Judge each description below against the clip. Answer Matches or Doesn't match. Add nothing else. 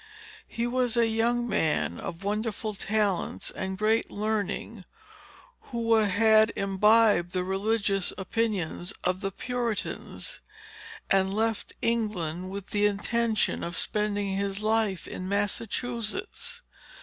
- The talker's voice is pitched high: Matches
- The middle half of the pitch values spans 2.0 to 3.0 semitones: Matches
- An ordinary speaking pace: Doesn't match